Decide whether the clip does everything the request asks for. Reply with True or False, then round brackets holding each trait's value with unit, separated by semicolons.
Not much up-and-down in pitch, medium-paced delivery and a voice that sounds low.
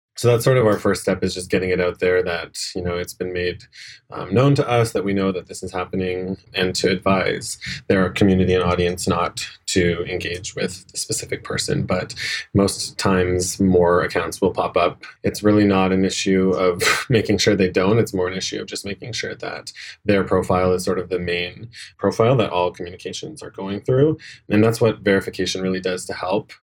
False (2.1 semitones; 210 wpm; 95 Hz)